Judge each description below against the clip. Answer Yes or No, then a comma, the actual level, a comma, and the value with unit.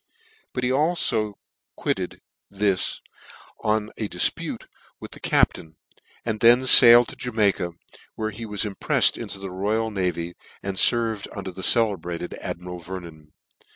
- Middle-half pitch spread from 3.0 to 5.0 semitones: Yes, average, 3.9 semitones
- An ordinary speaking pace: No, slow, 130 wpm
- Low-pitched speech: Yes, low, 105 Hz